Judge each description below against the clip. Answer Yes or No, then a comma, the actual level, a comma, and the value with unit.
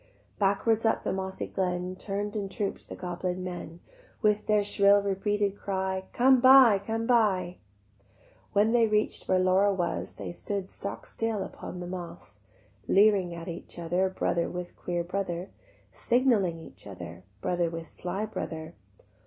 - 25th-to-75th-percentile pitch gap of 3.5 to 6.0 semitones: No, average, 2.8 semitones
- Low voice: No, high, 190 Hz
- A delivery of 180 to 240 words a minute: No, average, 150 wpm